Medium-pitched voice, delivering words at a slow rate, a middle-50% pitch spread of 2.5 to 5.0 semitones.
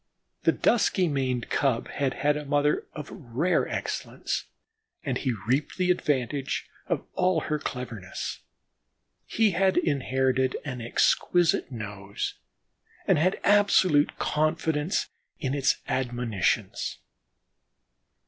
Yes: medium, 145 Hz; slow, 110 wpm; average, 4.3 semitones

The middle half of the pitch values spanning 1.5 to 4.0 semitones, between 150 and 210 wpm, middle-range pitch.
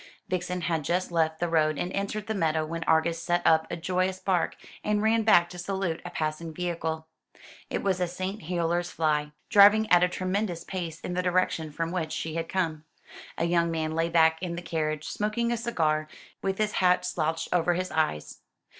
Yes: narrow, 2.4 semitones; average, 200 wpm; medium, 170 Hz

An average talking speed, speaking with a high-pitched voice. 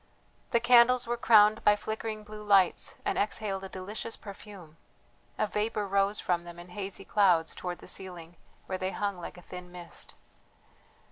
Yes: average, 165 wpm; high, 200 Hz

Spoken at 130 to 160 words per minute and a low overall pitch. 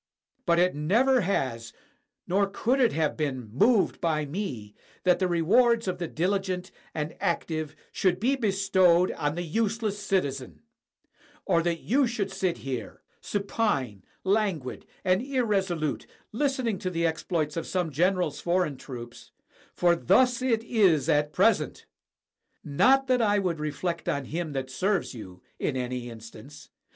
No: average, 150 wpm; medium, 175 Hz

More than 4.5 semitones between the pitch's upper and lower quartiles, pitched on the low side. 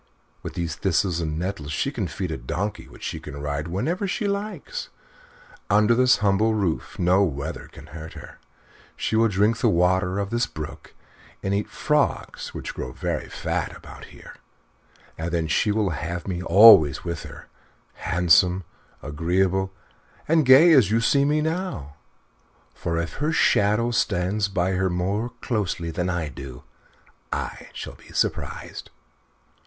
Yes: average, 5.2 semitones; very low, 95 Hz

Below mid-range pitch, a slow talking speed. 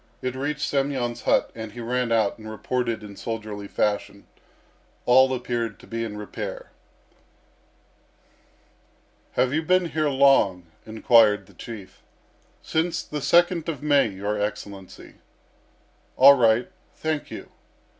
Yes: low, 120 Hz; slow, 125 wpm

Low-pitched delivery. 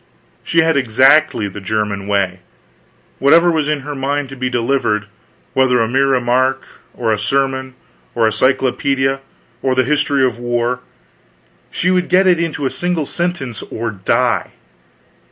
Yes: low, 130 Hz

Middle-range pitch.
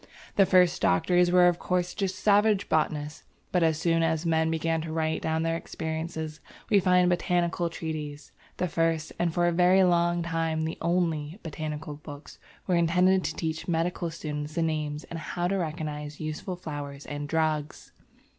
Yes: medium, 165 Hz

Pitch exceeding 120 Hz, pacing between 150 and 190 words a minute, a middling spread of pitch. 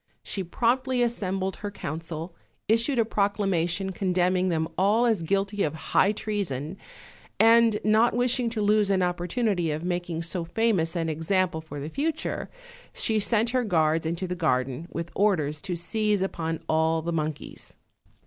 Yes: medium, 185 Hz; average, 160 wpm; average, 4.6 semitones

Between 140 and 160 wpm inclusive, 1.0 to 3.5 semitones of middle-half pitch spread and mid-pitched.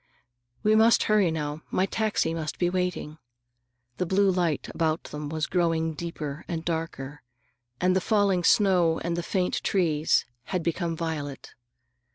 Yes: average, 150 wpm; narrow, 2.6 semitones; medium, 170 Hz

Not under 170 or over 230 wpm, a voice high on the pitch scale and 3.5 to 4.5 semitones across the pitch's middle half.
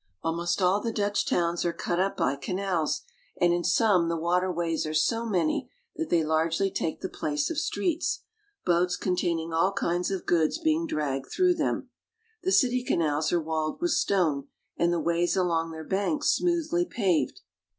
No: average, 175 wpm; medium, 175 Hz; average, 3.8 semitones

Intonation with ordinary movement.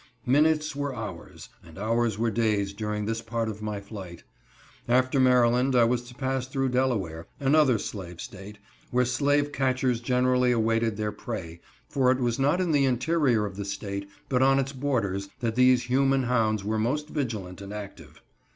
Yes: average, 3.8 semitones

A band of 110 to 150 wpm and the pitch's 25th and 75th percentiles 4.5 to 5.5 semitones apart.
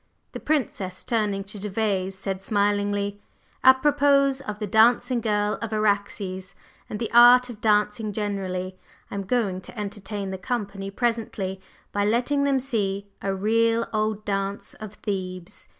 No: average, 145 wpm; average, 2.7 semitones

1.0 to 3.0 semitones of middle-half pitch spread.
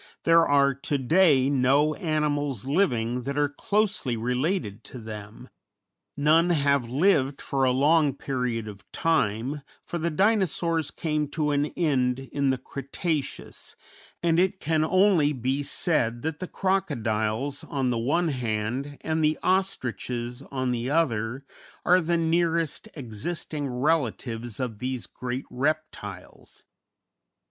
No: average, 4.5 semitones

